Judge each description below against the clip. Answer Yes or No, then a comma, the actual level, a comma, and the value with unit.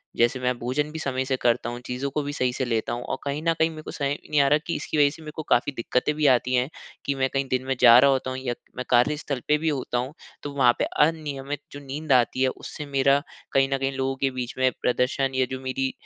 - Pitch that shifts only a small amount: Yes, narrow, 2.2 semitones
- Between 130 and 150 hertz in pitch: Yes, low, 135 Hz